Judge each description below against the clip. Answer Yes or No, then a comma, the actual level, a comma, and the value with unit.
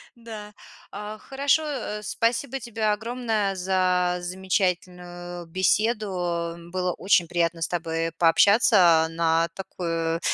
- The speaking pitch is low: No, medium, 185 Hz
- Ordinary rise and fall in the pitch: Yes, average, 3.8 semitones